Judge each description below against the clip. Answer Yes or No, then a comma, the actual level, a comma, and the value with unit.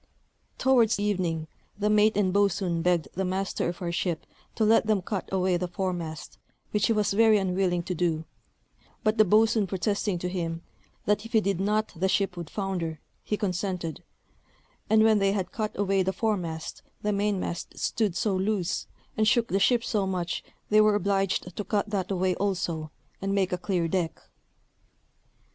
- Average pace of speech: Yes, average, 175 wpm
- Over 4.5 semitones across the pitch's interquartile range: No, average, 2.8 semitones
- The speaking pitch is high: Yes, high, 195 Hz